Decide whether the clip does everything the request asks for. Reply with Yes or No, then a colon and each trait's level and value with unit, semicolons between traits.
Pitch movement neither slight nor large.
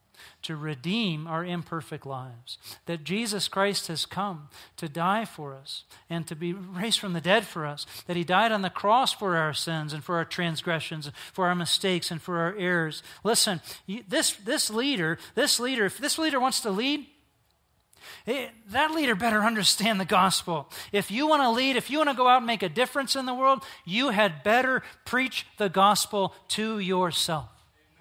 No: wide, 5.8 semitones